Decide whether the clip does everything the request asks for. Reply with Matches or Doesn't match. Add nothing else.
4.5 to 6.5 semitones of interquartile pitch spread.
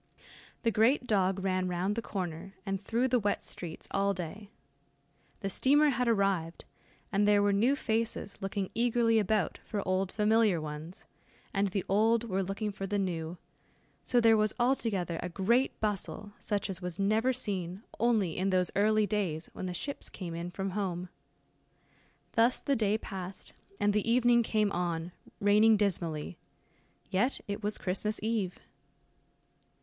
Doesn't match